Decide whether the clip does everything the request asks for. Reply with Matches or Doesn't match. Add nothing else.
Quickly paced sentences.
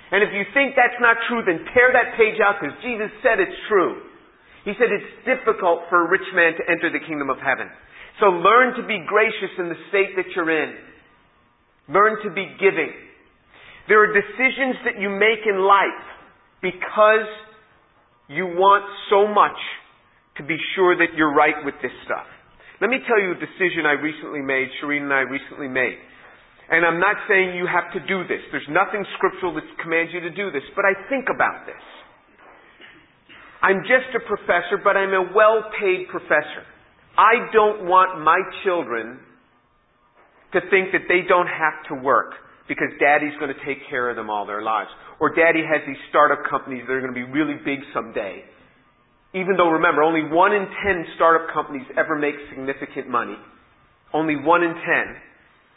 Doesn't match